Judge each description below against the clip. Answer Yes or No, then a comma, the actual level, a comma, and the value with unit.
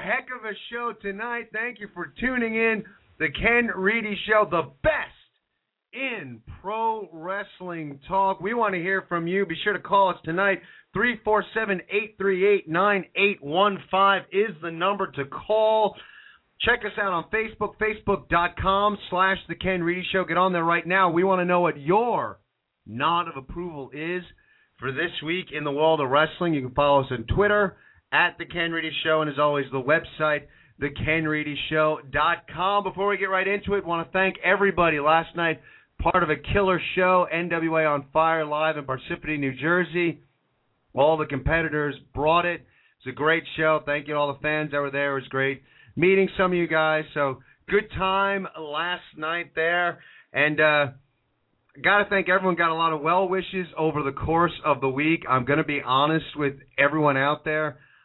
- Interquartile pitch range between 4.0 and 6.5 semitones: Yes, average, 4.5 semitones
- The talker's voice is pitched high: No, medium, 170 Hz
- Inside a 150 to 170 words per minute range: No, average, 180 wpm